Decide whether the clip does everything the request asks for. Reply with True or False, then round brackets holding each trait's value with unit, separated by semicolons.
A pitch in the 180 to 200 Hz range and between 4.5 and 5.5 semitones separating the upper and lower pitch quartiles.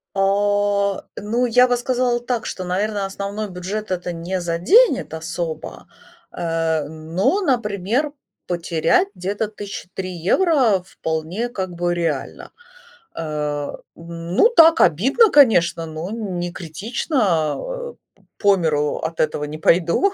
True (190 Hz; 5.2 semitones)